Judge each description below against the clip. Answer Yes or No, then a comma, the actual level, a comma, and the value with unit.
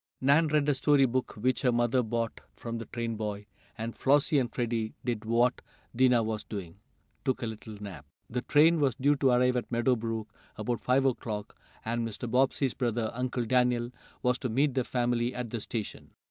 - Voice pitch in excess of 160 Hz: No, low, 120 Hz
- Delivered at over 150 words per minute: Yes, average, 190 wpm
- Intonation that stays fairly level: Yes, narrow, 2.3 semitones